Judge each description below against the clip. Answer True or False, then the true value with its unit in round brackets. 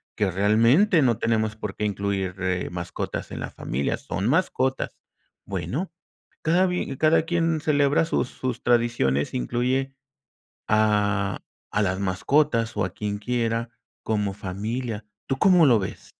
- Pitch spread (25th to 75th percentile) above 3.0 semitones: True (5.2 semitones)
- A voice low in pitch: True (115 Hz)